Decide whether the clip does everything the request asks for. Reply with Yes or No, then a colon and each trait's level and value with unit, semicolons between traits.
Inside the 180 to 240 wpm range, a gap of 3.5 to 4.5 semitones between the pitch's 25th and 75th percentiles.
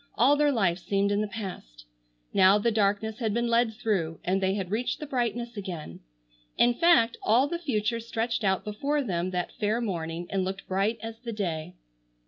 Yes: average, 190 wpm; average, 3.8 semitones